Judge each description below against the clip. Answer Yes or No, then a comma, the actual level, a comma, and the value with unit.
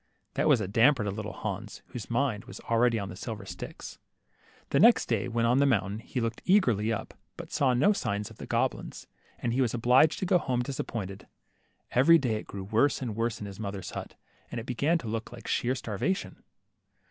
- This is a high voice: No, low, 115 Hz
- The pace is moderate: No, fast, 215 wpm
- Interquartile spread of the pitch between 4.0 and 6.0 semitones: No, average, 3.6 semitones